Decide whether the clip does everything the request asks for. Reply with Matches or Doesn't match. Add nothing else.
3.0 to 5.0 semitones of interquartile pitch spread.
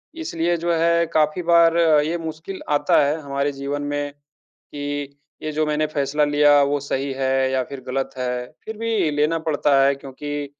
Doesn't match